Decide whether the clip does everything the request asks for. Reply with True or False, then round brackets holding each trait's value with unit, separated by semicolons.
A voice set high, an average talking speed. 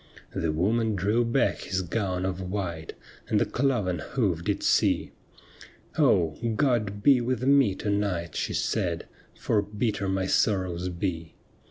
False (100 Hz; 155 wpm)